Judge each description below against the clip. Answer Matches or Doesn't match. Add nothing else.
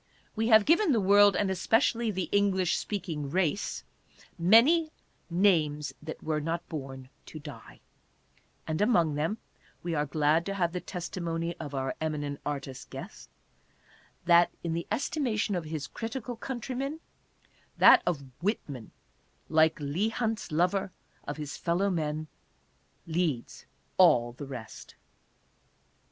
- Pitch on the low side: Doesn't match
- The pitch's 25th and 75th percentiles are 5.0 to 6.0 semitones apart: Matches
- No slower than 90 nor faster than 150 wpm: Matches